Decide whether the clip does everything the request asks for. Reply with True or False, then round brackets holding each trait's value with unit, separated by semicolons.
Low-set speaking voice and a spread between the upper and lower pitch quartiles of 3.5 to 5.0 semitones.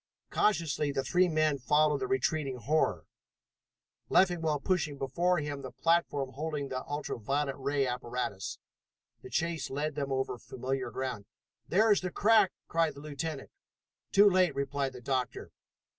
False (145 Hz; 3.8 semitones)